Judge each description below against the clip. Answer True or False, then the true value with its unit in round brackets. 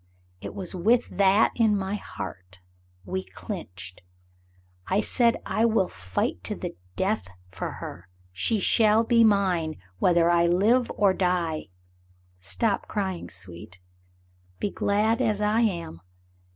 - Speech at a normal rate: False (130 wpm)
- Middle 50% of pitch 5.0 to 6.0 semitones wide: True (5.6 semitones)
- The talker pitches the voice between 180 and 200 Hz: True (190 Hz)